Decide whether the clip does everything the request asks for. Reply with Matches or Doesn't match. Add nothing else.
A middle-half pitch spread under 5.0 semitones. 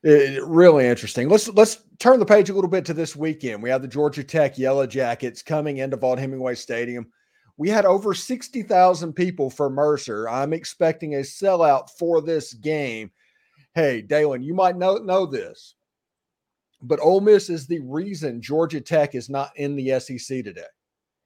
Doesn't match